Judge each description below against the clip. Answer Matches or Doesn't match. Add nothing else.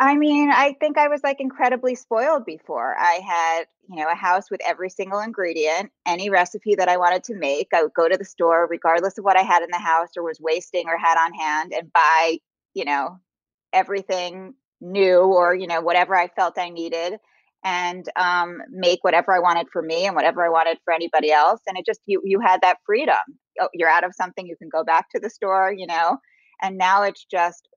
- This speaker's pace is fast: Matches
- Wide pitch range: Doesn't match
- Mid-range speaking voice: Matches